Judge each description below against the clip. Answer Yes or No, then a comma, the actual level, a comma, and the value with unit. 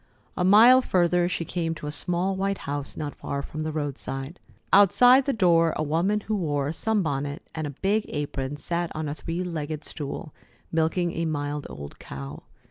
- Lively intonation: No, average, 3.9 semitones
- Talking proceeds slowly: No, average, 185 wpm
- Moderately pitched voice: Yes, medium, 160 Hz